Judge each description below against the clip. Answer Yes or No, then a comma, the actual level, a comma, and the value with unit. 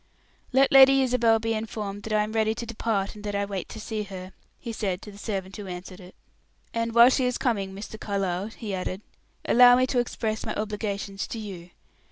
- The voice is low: No, high, 215 Hz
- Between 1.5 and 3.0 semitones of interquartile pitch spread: Yes, average, 2.7 semitones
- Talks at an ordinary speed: No, fast, 215 wpm